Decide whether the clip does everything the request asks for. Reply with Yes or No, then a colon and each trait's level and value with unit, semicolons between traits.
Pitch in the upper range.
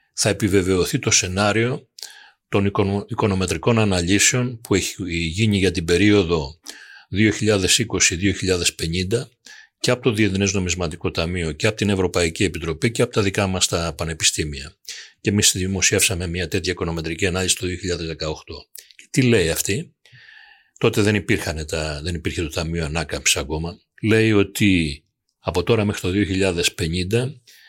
No: very low, 95 Hz